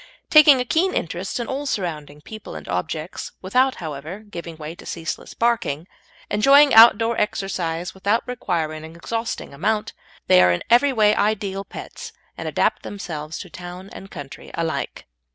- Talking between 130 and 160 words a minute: Yes, average, 155 wpm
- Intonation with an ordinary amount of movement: No, wide, 6.0 semitones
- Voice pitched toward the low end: No, high, 190 Hz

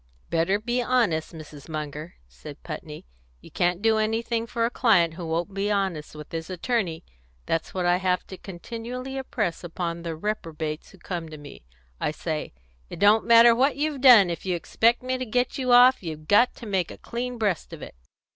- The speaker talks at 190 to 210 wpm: Yes, average, 195 wpm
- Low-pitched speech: No, high, 195 Hz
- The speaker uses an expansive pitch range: Yes, wide, 6.1 semitones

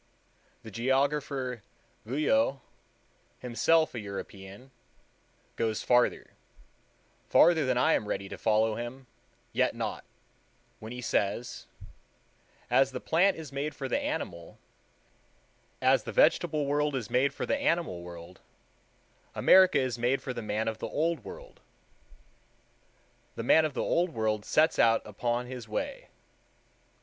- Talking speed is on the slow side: Yes, slow, 130 wpm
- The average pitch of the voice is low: Yes, low, 130 Hz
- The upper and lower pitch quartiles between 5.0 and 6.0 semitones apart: Yes, average, 5.3 semitones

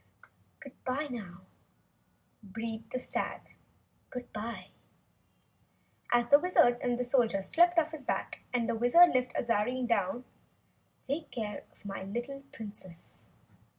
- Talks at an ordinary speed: No, slow, 115 wpm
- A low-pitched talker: No, high, 240 Hz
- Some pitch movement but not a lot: Yes, average, 3.9 semitones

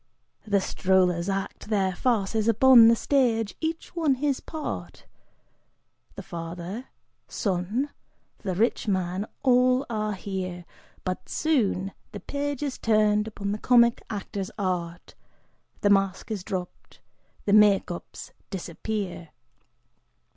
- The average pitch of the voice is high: Yes, high, 205 Hz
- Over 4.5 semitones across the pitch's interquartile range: No, average, 4.2 semitones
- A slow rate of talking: Yes, slow, 120 wpm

